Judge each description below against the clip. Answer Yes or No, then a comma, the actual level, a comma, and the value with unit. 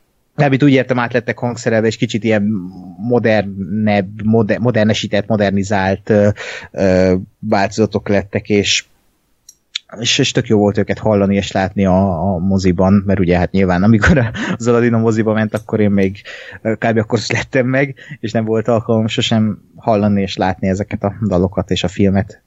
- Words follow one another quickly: Yes, fast, 160 wpm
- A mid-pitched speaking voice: No, low, 105 Hz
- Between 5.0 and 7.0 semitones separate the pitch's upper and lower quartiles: No, average, 2.7 semitones